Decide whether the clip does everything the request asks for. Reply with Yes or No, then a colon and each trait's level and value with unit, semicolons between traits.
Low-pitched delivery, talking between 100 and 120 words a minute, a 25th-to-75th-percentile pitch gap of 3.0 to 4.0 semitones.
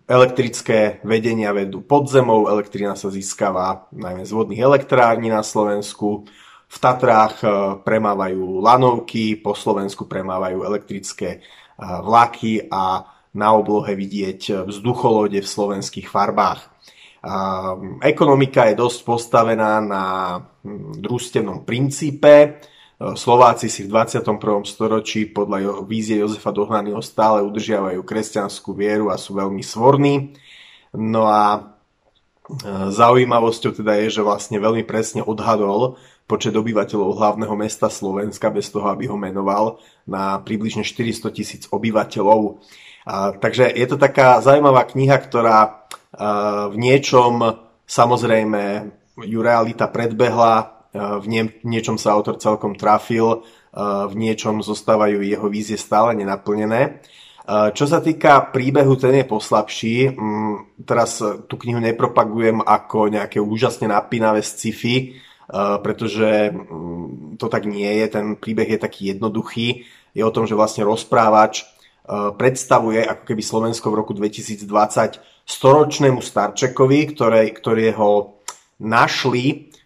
No: low, 110 Hz; average, 115 wpm; narrow, 2.4 semitones